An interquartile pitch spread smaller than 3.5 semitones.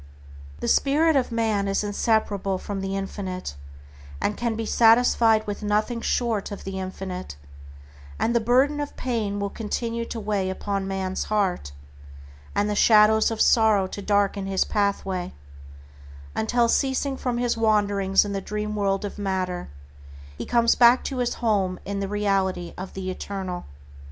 Yes: average, 2.9 semitones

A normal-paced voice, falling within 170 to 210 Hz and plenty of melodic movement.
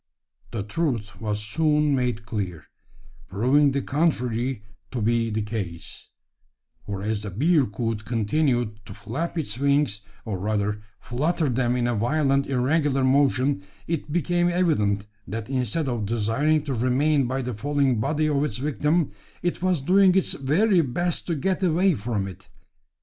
No: average, 150 wpm; low, 130 Hz; wide, 5.7 semitones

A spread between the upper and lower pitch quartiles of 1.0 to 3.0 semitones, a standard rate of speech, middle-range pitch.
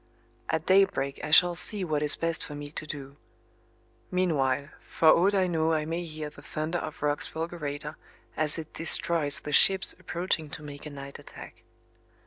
Yes: average, 2.7 semitones; average, 175 wpm; medium, 155 Hz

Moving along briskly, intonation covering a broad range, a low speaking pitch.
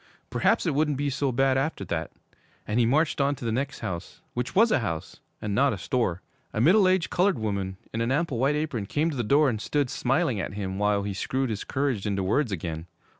Yes: fast, 230 wpm; wide, 6.0 semitones; low, 125 Hz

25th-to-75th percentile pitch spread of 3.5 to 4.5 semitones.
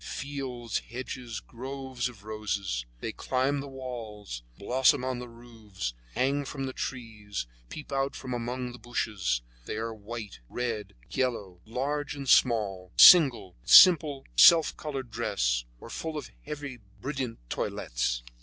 Yes: average, 4.2 semitones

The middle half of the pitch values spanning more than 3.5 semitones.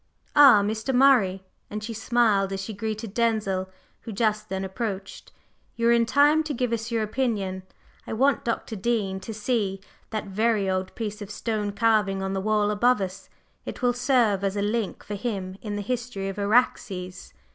No: average, 3.2 semitones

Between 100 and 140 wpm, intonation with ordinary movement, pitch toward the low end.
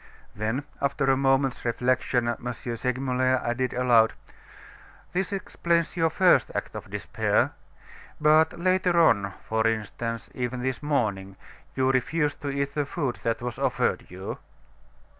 Yes: slow, 135 wpm; average, 3.8 semitones; low, 130 Hz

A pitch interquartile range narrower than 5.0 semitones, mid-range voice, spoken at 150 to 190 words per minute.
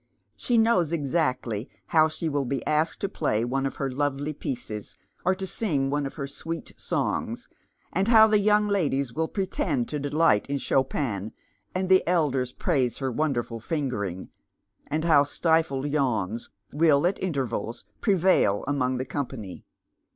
Yes: average, 4.5 semitones; medium, 145 Hz; average, 155 wpm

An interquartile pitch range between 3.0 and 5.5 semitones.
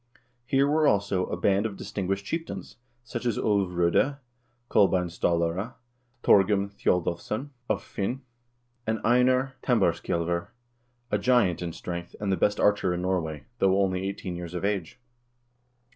Yes: average, 4.1 semitones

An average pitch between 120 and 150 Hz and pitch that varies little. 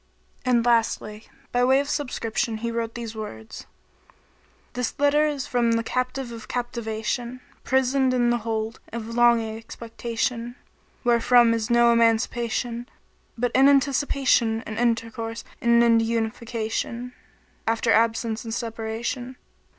No: high, 235 Hz; narrow, 1.5 semitones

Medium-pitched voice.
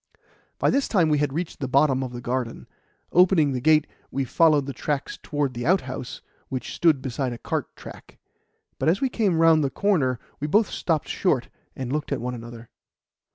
Yes: medium, 145 Hz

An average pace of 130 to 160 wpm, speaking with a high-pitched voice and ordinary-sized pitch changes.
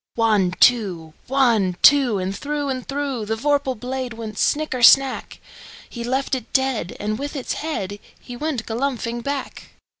Yes: average, 140 wpm; high, 245 Hz; average, 4.1 semitones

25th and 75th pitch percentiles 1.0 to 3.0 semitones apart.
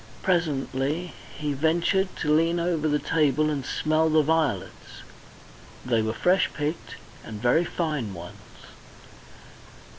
No: average, 3.6 semitones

